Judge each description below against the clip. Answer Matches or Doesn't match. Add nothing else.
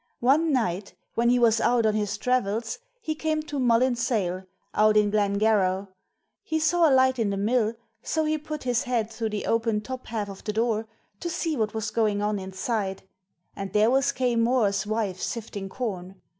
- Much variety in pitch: Doesn't match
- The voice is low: Doesn't match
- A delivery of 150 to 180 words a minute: Doesn't match